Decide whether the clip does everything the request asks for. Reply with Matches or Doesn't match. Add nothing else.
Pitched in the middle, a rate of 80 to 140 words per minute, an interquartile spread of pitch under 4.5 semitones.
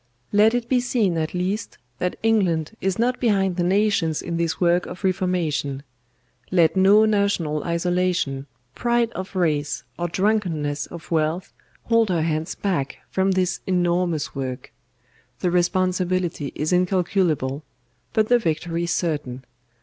Matches